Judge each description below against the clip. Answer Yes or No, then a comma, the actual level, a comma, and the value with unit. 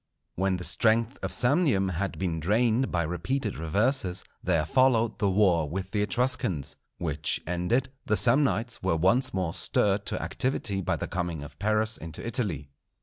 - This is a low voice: Yes, low, 100 Hz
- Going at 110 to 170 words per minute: Yes, average, 160 wpm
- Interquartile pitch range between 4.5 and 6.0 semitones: Yes, average, 5.2 semitones